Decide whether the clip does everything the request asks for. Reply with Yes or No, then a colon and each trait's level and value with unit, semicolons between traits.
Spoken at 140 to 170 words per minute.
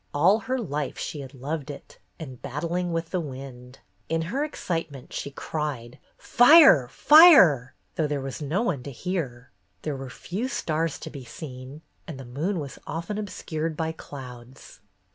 Yes: average, 160 wpm